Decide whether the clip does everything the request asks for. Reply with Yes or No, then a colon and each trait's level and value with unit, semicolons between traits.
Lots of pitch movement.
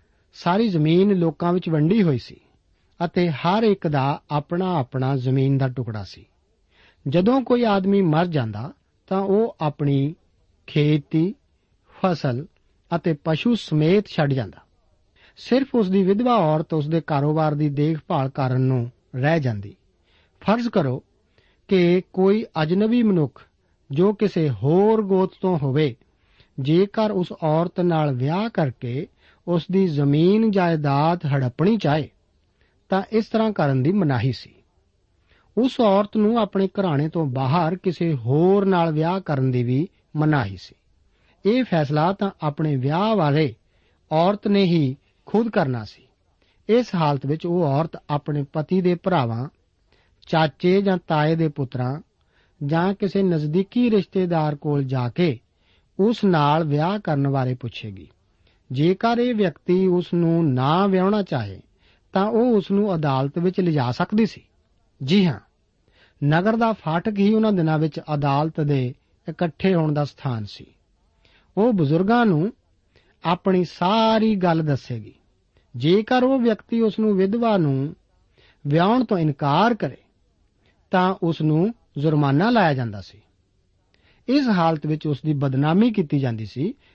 Yes: wide, 6.7 semitones